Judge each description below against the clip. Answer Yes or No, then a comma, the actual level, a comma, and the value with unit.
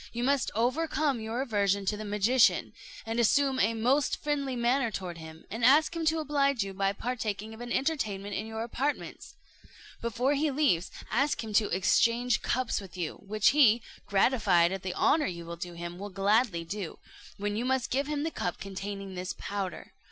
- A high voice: Yes, high, 225 Hz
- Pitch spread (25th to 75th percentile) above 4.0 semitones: Yes, average, 5.1 semitones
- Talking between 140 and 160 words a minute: No, average, 185 wpm